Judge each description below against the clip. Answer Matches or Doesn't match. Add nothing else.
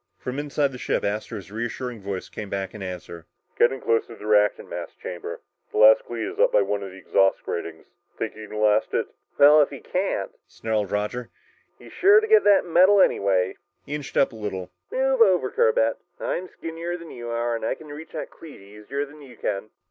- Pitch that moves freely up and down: Matches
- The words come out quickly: Matches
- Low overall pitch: Matches